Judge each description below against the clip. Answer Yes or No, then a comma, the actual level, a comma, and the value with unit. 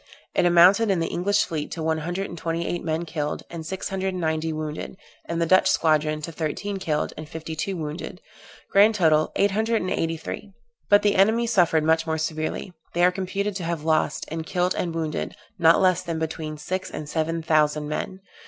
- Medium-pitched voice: Yes, medium, 165 Hz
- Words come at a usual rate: No, fast, 210 wpm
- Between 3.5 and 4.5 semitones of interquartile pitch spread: No, average, 3.0 semitones